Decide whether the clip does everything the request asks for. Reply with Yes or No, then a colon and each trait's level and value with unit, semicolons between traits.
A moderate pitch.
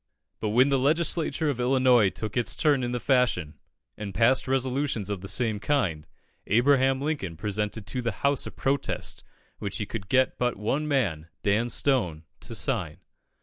No: low, 120 Hz